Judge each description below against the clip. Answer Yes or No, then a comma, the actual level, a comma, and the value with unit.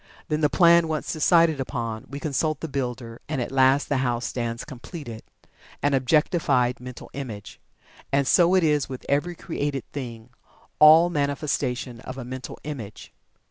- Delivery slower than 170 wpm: Yes, average, 155 wpm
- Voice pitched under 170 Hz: Yes, medium, 140 Hz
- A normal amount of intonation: Yes, average, 3.6 semitones